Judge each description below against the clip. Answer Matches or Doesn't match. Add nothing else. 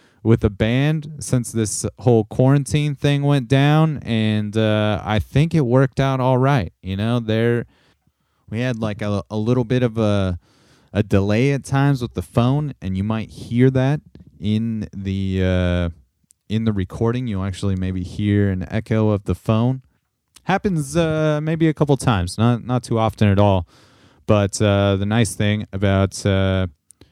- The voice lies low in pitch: Matches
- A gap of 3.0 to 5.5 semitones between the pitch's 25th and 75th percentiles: Matches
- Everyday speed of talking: Matches